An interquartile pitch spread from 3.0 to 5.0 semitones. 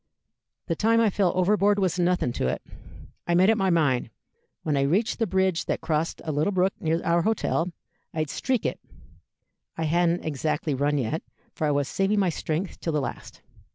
Yes: average, 4.1 semitones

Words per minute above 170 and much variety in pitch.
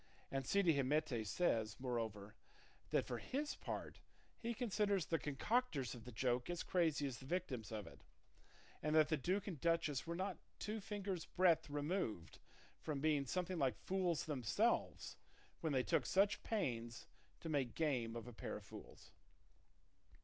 No: average, 160 wpm; wide, 6.8 semitones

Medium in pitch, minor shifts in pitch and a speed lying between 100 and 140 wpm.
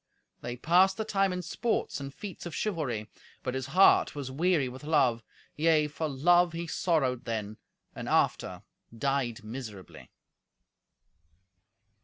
No: medium, 145 Hz; wide, 5.6 semitones; slow, 135 wpm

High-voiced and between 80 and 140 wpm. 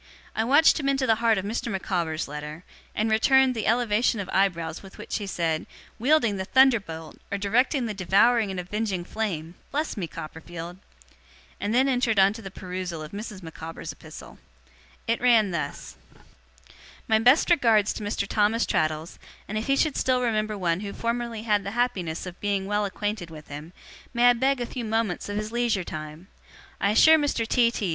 No: high, 210 Hz; average, 185 wpm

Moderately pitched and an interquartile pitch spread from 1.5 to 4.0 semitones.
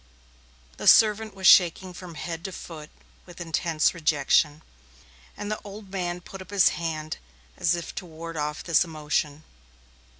Yes: medium, 170 Hz; average, 3.1 semitones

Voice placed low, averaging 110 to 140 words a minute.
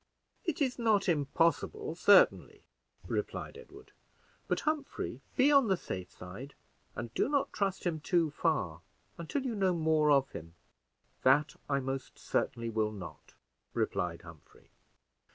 No: medium, 155 Hz; slow, 135 wpm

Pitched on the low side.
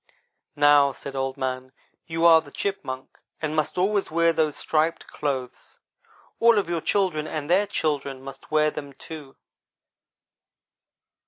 No: medium, 155 Hz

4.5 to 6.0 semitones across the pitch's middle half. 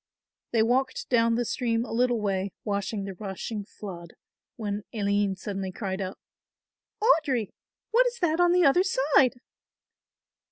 Yes: average, 5.2 semitones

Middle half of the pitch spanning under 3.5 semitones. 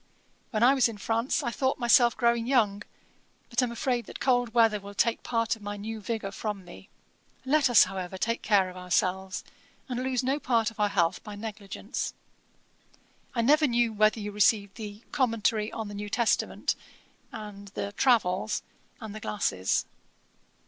Yes: average, 2.8 semitones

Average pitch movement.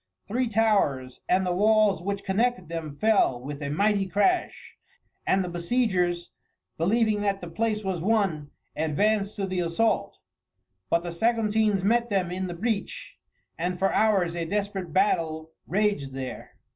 Yes: average, 4.1 semitones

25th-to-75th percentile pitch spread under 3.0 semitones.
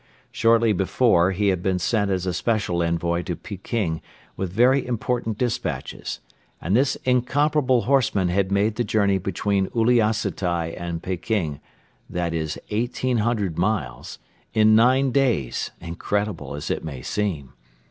No: average, 5.2 semitones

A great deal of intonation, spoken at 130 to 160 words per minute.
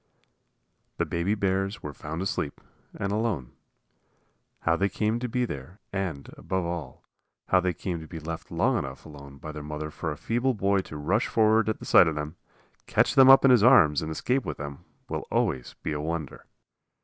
No: wide, 5.9 semitones; average, 195 wpm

